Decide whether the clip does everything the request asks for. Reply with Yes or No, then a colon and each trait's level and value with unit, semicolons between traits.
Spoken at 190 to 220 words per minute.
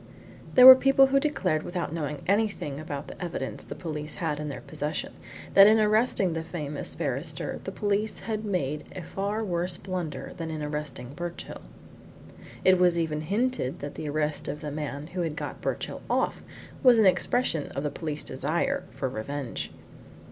No: average, 175 wpm